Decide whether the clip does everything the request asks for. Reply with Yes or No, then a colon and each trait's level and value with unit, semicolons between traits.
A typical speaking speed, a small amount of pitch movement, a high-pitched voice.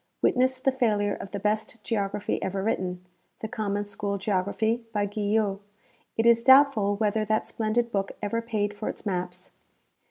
Yes: average, 165 wpm; narrow, 2.2 semitones; high, 210 Hz